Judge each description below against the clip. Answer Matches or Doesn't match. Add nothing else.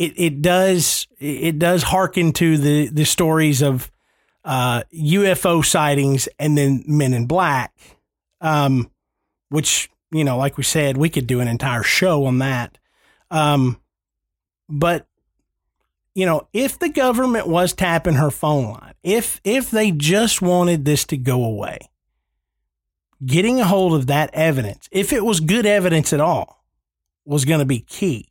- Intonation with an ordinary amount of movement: Matches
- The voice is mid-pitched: Matches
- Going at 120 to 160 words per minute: Matches